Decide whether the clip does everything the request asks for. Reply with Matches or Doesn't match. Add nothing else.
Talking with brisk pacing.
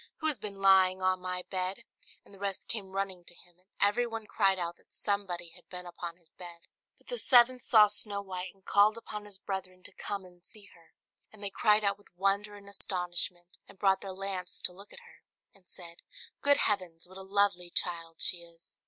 Matches